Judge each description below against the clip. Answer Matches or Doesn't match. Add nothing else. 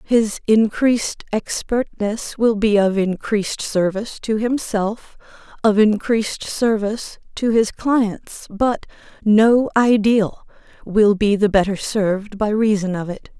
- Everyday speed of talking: Doesn't match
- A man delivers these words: Doesn't match